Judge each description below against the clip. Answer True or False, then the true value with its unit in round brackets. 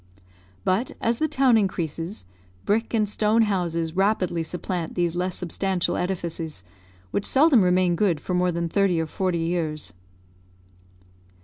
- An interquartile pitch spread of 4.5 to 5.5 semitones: False (3.6 semitones)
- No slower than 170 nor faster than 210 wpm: False (135 wpm)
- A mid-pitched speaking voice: True (180 Hz)